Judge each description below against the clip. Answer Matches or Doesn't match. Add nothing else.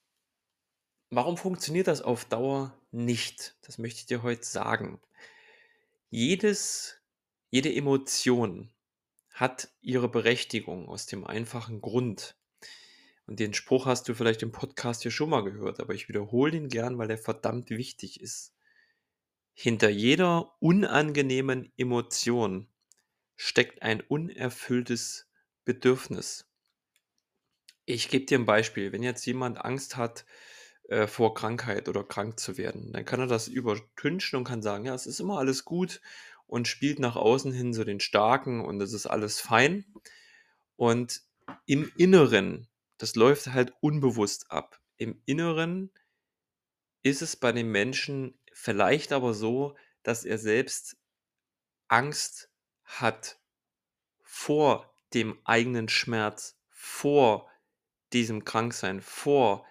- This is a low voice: Matches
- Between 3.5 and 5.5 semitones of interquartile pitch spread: Matches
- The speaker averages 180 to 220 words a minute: Doesn't match